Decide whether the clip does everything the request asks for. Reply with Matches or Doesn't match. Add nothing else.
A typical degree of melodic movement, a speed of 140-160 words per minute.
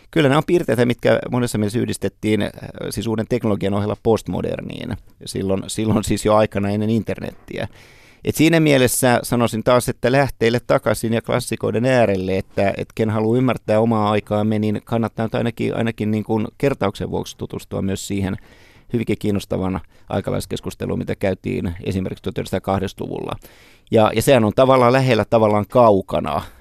Matches